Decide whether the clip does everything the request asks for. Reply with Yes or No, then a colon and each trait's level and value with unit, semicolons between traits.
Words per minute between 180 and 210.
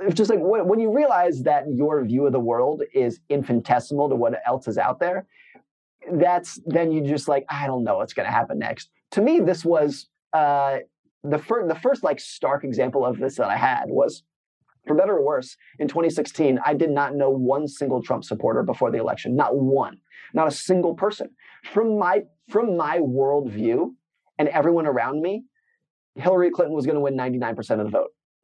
Yes: average, 195 wpm